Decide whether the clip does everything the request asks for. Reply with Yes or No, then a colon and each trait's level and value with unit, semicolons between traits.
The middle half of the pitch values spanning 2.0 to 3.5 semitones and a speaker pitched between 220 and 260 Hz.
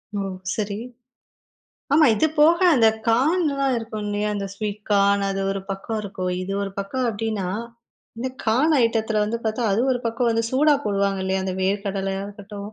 No: average, 2.9 semitones; high, 210 Hz